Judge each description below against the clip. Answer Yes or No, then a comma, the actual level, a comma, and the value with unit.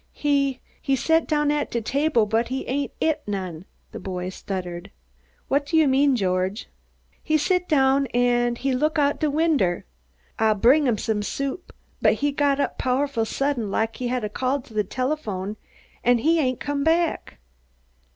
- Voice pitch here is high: Yes, very high, 265 Hz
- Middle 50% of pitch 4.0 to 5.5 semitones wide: Yes, average, 4.8 semitones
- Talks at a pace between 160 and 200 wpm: Yes, average, 170 wpm